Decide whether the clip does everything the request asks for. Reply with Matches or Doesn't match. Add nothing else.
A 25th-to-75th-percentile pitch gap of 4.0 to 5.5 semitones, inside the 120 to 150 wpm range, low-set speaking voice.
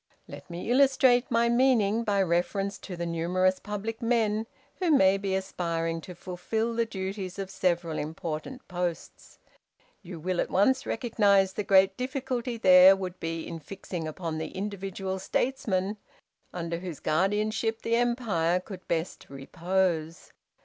Doesn't match